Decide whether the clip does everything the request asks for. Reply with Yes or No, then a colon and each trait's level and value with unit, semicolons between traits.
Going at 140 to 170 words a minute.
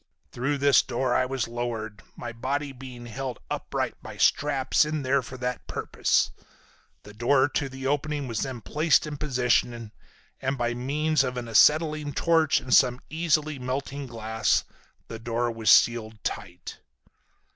Yes: average, 155 wpm